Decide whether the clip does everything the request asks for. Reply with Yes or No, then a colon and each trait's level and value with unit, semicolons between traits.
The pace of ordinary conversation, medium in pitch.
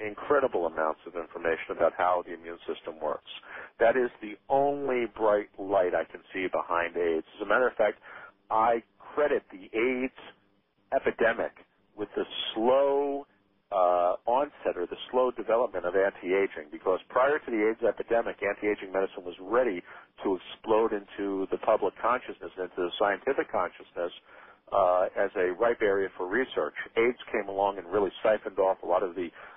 No: average, 160 wpm; low, 105 Hz